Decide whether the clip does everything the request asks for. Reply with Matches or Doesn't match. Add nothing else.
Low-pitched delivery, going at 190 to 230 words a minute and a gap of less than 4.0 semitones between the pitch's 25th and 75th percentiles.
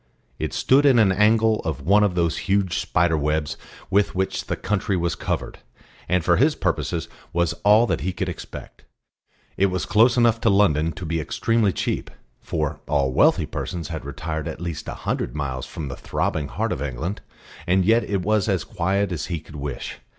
Doesn't match